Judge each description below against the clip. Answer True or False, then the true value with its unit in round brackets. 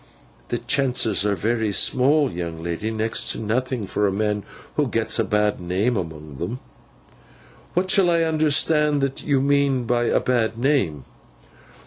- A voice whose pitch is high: False (115 Hz)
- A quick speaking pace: False (145 wpm)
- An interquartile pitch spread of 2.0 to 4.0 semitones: False (5.5 semitones)